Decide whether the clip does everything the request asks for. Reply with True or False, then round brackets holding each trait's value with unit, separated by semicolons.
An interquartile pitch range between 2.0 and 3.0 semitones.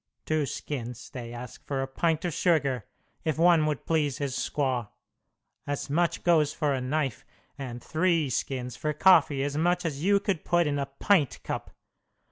False (3.6 semitones)